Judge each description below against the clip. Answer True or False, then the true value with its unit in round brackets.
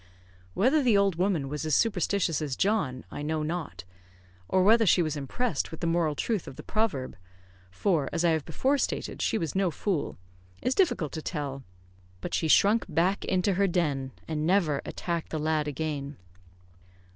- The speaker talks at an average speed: True (180 wpm)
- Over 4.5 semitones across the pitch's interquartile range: True (4.9 semitones)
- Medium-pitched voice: True (165 Hz)